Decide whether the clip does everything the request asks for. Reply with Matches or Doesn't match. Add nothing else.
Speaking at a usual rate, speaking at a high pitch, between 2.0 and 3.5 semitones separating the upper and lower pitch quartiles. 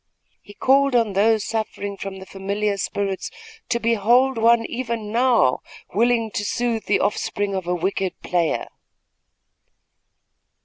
Doesn't match